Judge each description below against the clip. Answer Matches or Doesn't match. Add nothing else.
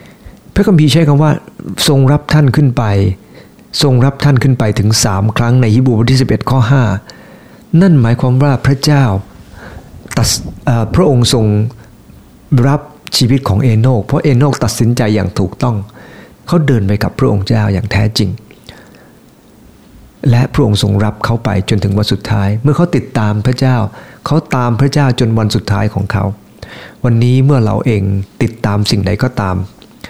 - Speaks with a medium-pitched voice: Doesn't match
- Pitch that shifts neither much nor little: Matches